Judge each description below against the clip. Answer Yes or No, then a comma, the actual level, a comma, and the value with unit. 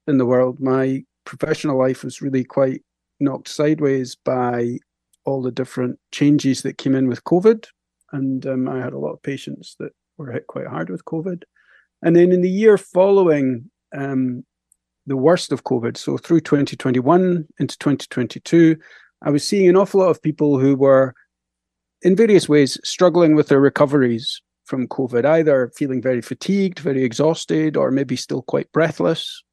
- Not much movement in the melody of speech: No, average, 3.8 semitones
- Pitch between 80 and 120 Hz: No, medium, 140 Hz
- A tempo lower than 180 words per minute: Yes, average, 165 wpm